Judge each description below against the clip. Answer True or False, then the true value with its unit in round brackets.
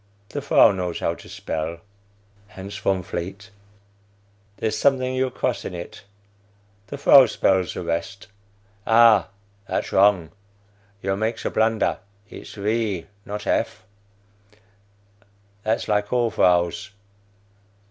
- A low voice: True (105 Hz)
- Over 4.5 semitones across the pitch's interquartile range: False (3.6 semitones)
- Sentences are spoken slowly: True (120 wpm)